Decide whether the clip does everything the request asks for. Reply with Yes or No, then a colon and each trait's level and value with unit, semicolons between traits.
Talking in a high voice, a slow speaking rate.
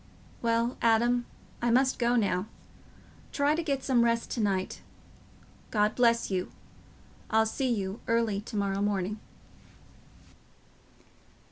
Yes: high, 230 Hz; slow, 120 wpm